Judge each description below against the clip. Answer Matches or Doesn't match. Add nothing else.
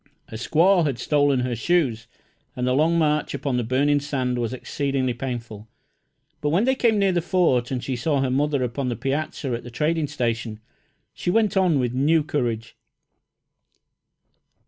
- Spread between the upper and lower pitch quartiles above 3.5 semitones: Matches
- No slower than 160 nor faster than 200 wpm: Matches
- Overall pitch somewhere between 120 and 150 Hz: Matches